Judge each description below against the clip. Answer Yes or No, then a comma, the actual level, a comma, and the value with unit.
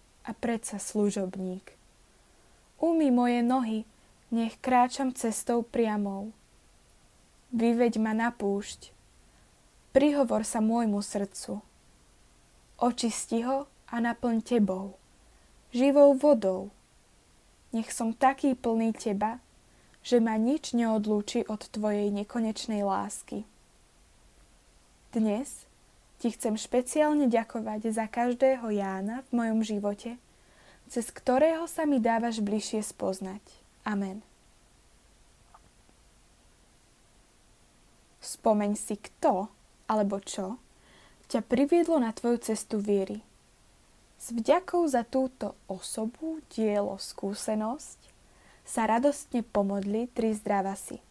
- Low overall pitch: No, high, 225 Hz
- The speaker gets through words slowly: Yes, slow, 95 wpm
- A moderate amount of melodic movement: Yes, average, 3.1 semitones